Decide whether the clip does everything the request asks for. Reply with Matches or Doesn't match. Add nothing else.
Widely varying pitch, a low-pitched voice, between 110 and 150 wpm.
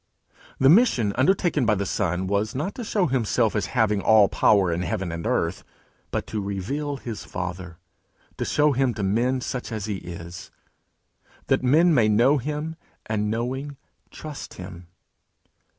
Doesn't match